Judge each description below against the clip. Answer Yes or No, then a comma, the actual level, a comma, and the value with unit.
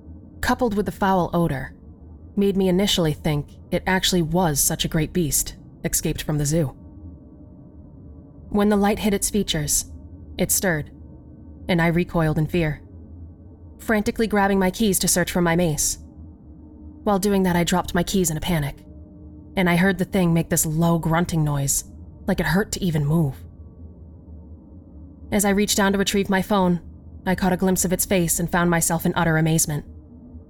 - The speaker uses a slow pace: No, average, 175 wpm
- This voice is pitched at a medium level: Yes, medium, 165 Hz